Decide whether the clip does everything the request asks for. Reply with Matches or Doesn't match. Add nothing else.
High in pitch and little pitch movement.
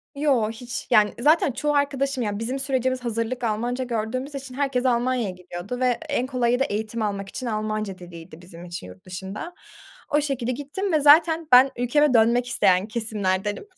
Doesn't match